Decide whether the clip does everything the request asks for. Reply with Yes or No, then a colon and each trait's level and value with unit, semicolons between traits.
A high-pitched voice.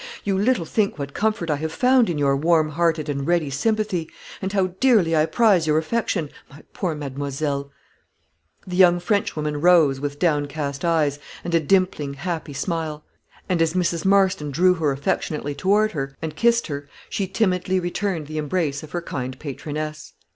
No: medium, 160 Hz